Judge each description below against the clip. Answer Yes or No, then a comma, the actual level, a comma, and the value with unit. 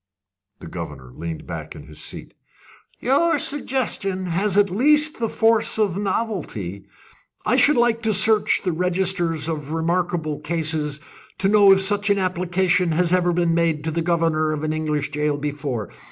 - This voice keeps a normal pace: Yes, average, 165 wpm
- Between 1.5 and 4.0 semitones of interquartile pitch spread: No, average, 4.9 semitones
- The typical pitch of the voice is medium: Yes, medium, 175 Hz